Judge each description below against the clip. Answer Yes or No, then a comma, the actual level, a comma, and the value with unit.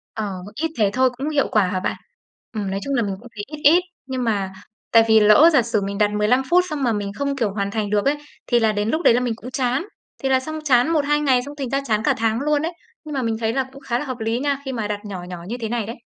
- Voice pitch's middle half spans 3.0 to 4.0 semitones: No, average, 4.8 semitones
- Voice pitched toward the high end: Yes, high, 240 Hz